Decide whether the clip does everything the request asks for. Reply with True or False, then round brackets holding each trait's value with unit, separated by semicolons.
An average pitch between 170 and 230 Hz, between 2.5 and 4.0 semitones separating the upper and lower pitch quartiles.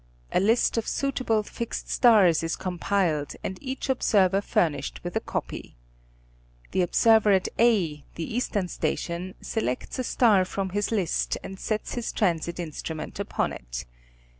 False (190 Hz; 4.7 semitones)